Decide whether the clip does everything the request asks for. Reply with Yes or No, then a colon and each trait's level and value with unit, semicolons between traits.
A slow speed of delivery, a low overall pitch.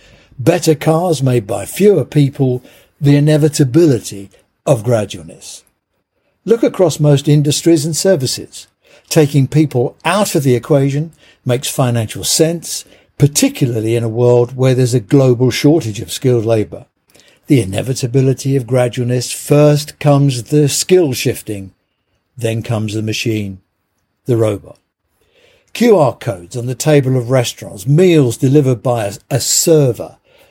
Yes: slow, 125 wpm; low, 130 Hz